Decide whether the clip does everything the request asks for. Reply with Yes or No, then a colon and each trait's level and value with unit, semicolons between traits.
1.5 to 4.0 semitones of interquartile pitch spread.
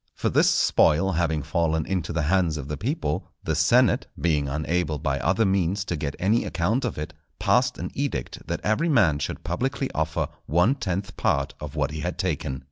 No: average, 4.5 semitones